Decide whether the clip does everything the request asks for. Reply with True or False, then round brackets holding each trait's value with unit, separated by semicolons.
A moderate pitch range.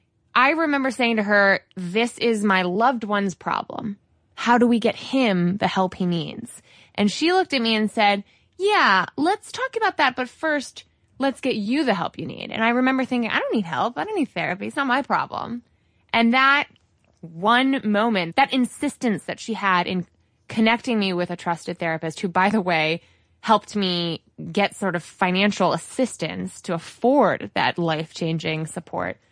False (5.9 semitones)